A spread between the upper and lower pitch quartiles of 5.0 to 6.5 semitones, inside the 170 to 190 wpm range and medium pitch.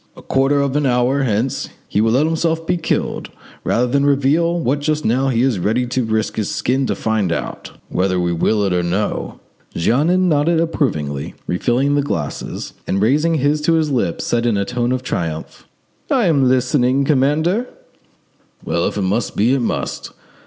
No: average, 5.3 semitones; average, 180 wpm; low, 130 Hz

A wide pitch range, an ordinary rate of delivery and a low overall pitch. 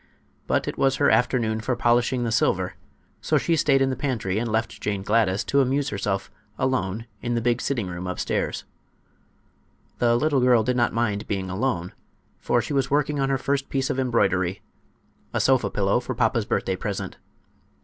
No: average, 4.3 semitones; average, 180 wpm; low, 120 Hz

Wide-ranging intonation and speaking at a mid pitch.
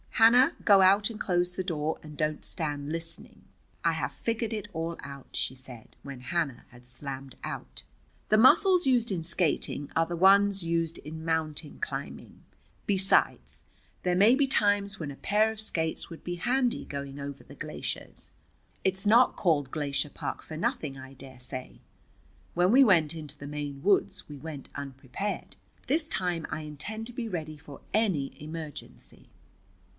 Yes: wide, 6.0 semitones; medium, 165 Hz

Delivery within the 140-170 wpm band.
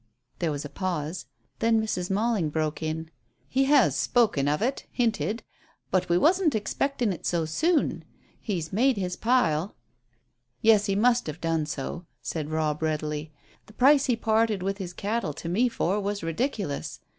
Yes: average, 165 wpm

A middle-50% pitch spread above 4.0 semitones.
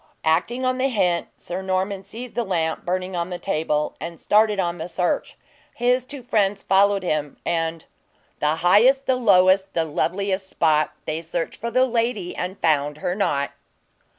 Yes: average, 4.5 semitones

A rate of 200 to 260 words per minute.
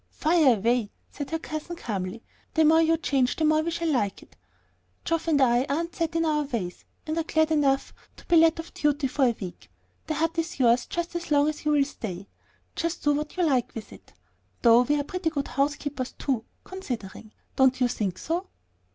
Yes: fast, 205 wpm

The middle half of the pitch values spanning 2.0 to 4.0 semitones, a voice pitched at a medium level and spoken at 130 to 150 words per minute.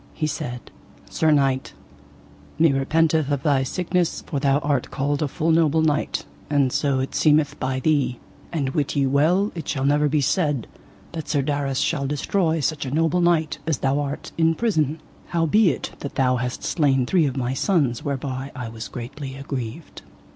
No: average, 3.0 semitones; medium, 145 Hz; average, 175 wpm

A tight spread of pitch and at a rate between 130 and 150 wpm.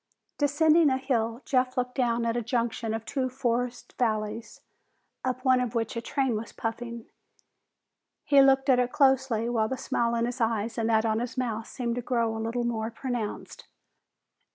No: narrow, 2.2 semitones; average, 180 wpm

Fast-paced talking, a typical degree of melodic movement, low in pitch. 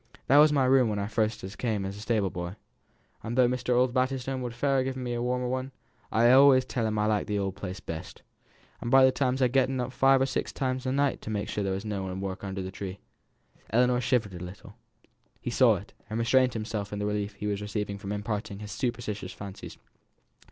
Yes: fast, 230 wpm; average, 4.1 semitones; low, 115 Hz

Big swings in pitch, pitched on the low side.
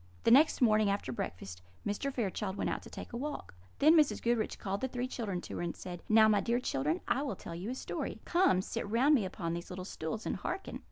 No: wide, 5.7 semitones; high, 215 Hz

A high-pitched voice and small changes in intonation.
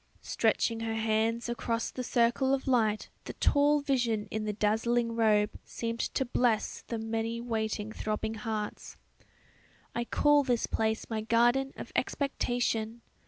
Yes: high, 230 Hz; narrow, 1.7 semitones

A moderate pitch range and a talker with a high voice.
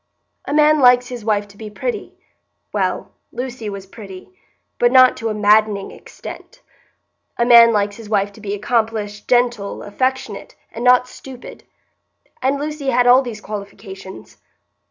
Yes: average, 3.5 semitones; high, 230 Hz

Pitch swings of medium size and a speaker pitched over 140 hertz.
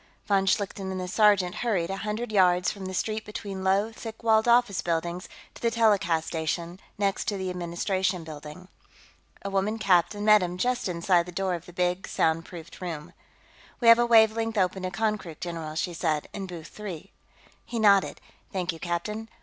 Yes: average, 3.4 semitones; high, 190 Hz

